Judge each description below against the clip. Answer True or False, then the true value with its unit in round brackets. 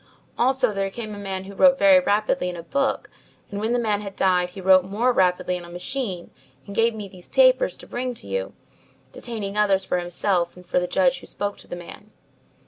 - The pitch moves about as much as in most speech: True (4.8 semitones)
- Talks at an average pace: False (220 wpm)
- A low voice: False (200 Hz)